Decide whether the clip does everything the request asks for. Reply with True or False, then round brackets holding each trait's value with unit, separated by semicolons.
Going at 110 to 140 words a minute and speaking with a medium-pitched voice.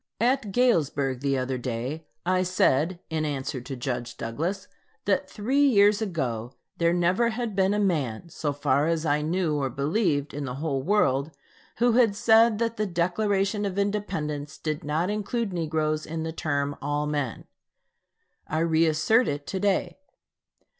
False (160 wpm; 160 Hz)